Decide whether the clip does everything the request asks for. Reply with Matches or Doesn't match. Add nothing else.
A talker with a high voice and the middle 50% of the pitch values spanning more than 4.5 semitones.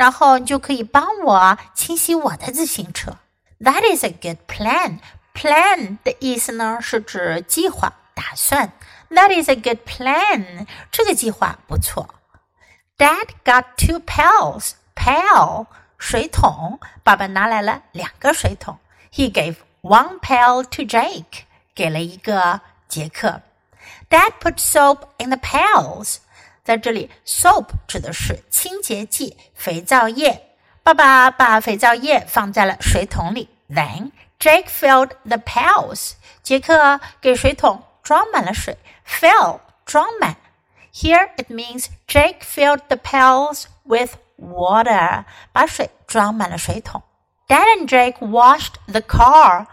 Matches